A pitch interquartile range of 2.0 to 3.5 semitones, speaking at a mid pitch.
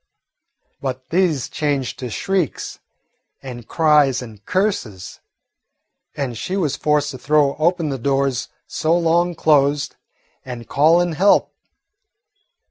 No: average, 4.2 semitones; medium, 145 Hz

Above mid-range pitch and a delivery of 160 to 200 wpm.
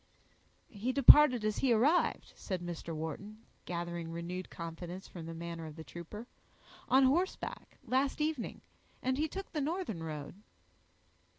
No: high, 200 Hz; average, 140 wpm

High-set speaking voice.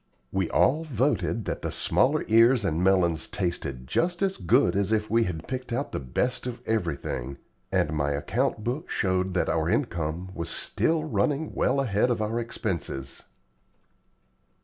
No: low, 105 Hz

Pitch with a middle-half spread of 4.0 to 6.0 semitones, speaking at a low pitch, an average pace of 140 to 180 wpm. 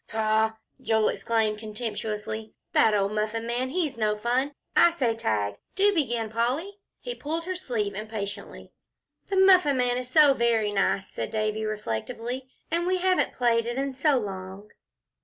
No: average, 4.4 semitones; high, 230 Hz; average, 160 wpm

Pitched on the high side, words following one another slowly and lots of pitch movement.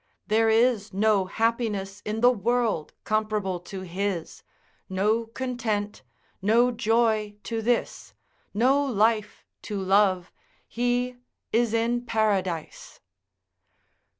No: high, 220 Hz; slow, 100 wpm; average, 2.8 semitones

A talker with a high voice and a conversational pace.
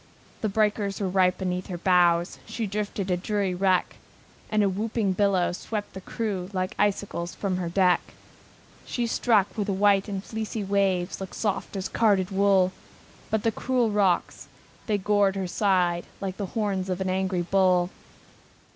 Yes: high, 195 Hz; average, 165 wpm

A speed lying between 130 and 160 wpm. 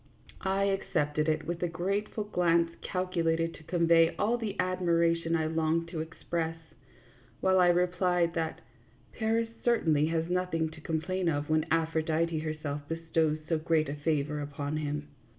Yes: average, 155 wpm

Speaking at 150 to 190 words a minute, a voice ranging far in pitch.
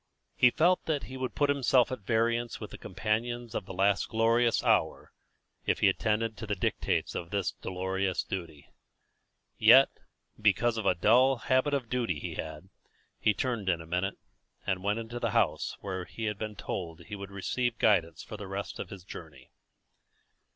No: average, 180 wpm; average, 4.1 semitones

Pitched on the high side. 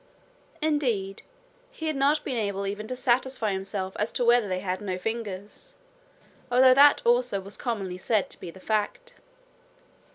Yes: high, 220 Hz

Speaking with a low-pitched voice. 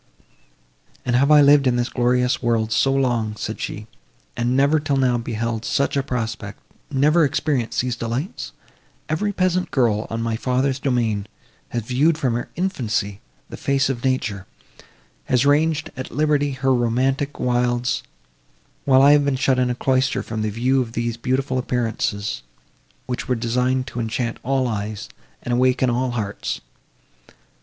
Yes: low, 125 Hz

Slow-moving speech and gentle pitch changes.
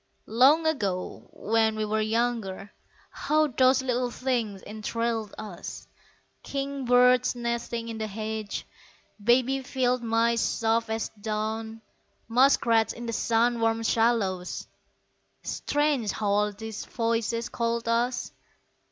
Yes: slow, 115 wpm; narrow, 2.1 semitones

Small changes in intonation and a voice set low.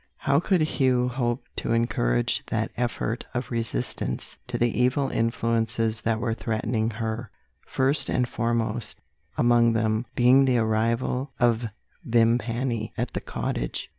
Yes: narrow, 1.7 semitones; low, 115 Hz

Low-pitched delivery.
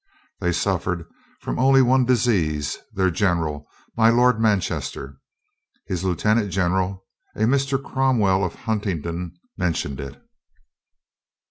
Yes: very low, 95 Hz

